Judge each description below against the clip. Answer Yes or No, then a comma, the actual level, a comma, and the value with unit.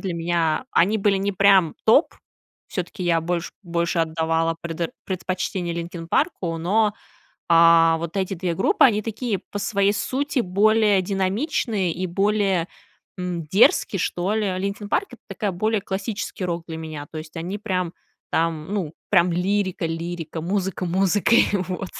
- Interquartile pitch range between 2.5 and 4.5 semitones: Yes, average, 3.2 semitones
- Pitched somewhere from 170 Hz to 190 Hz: Yes, medium, 185 Hz